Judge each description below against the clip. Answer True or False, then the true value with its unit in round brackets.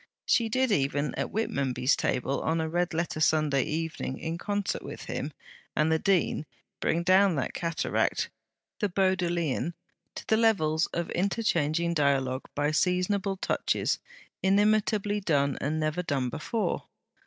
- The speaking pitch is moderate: True (170 Hz)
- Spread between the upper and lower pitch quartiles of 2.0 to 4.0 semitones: False (4.5 semitones)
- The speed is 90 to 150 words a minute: True (140 wpm)